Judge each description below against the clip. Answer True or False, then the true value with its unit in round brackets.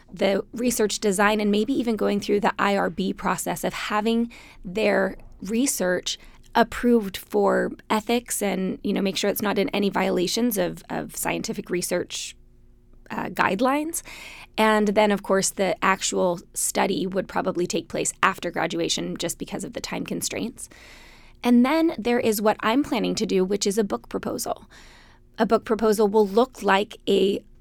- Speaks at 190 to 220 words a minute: False (160 wpm)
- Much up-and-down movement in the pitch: False (2.9 semitones)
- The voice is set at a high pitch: True (210 Hz)